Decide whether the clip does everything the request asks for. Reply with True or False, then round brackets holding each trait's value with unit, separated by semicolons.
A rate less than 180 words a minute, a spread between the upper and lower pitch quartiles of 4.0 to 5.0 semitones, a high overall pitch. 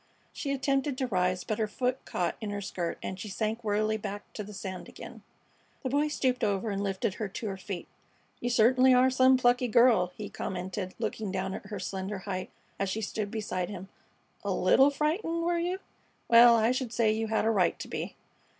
False (205 wpm; 4.6 semitones; 215 Hz)